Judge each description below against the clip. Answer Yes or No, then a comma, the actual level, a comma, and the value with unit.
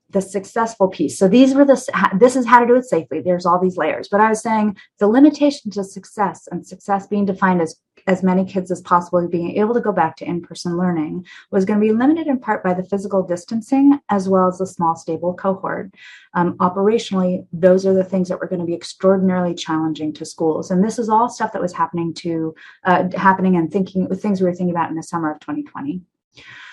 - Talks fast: Yes, fast, 230 wpm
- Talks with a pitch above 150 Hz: Yes, medium, 185 Hz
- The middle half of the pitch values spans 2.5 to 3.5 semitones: Yes, average, 3.0 semitones